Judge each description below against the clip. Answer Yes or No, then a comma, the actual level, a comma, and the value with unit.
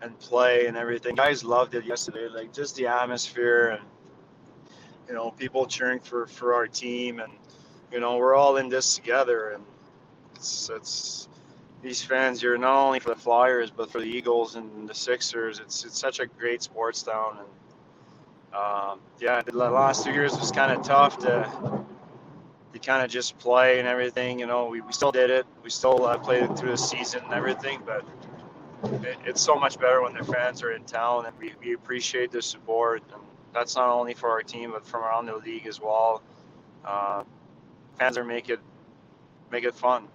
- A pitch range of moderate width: No, narrow, 2.0 semitones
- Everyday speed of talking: Yes, average, 190 wpm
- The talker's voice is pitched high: No, low, 120 Hz